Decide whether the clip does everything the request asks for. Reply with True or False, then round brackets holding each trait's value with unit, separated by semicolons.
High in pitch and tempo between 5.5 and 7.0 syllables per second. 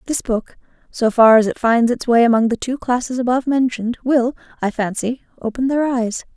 True (240 Hz; 5.6 syllables/s)